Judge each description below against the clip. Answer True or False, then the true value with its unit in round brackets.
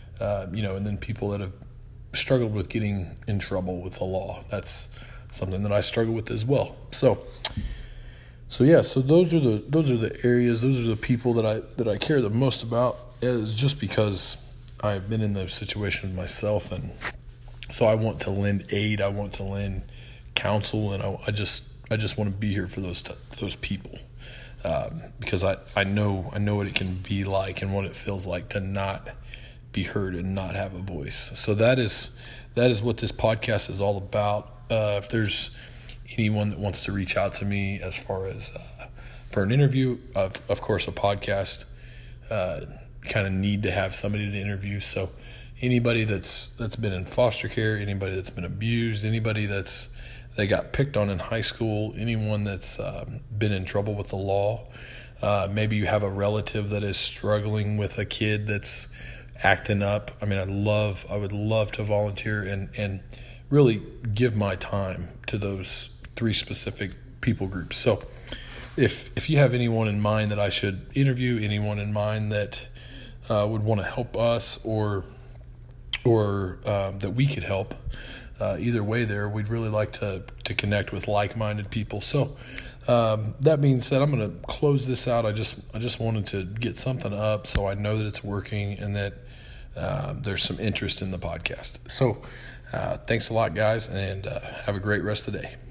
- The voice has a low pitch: True (105 Hz)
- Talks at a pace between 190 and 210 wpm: True (195 wpm)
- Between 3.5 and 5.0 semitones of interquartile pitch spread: False (3.1 semitones)